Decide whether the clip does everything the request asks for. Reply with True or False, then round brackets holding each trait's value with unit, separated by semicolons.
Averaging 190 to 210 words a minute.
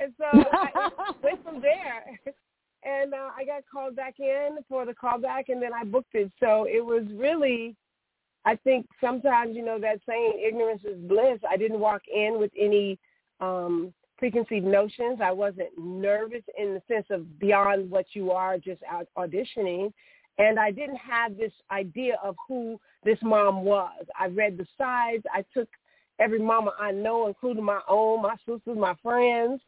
False (175 wpm)